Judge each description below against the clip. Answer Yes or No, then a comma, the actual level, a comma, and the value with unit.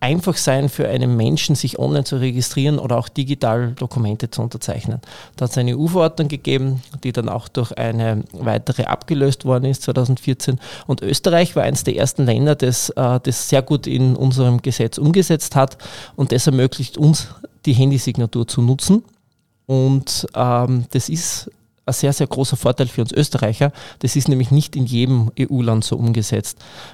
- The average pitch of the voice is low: Yes, low, 130 Hz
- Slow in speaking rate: No, average, 165 wpm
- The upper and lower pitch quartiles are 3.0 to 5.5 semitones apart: No, narrow, 2.6 semitones